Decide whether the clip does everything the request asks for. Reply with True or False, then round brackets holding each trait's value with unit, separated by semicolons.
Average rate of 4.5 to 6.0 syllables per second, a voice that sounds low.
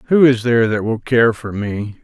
True (4.9 syllables/s; 115 Hz)